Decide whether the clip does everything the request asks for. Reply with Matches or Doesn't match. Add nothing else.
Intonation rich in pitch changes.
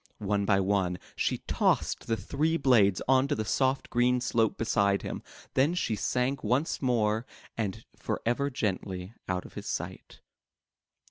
Doesn't match